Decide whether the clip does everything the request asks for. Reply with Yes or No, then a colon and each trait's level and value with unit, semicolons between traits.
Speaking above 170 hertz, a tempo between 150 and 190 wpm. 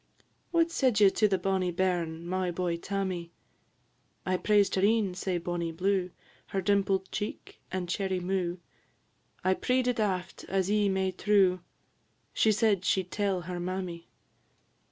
Yes: high, 190 Hz; average, 155 wpm